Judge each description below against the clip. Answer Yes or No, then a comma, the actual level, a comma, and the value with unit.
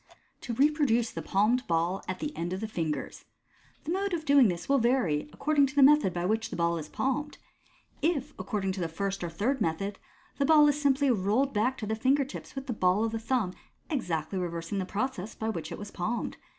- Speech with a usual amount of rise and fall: No, wide, 7.0 semitones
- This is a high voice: Yes, high, 220 Hz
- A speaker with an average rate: No, fast, 230 wpm